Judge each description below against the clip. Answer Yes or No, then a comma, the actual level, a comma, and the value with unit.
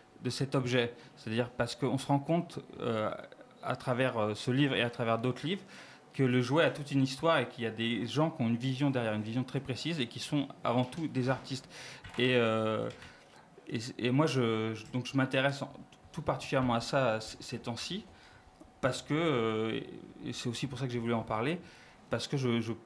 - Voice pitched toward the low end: Yes, low, 125 Hz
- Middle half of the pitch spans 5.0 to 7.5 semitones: No, average, 3.1 semitones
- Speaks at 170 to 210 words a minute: No, fast, 220 wpm